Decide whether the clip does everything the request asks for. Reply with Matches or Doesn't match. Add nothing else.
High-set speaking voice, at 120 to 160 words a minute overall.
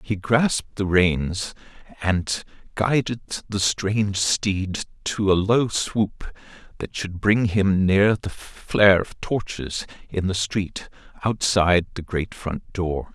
Doesn't match